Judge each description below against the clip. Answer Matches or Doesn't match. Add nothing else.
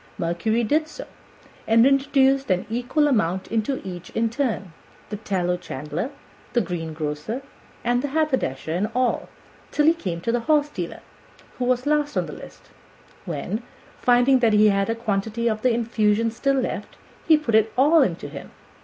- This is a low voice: Doesn't match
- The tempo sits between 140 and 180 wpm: Matches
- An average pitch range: Doesn't match